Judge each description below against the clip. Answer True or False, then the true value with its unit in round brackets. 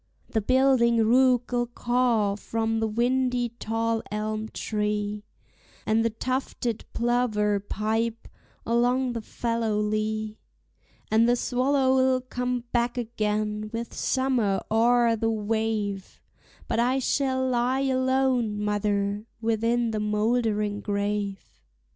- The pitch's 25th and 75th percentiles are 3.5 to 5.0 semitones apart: False (2.7 semitones)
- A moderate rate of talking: False (110 wpm)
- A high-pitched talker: True (230 Hz)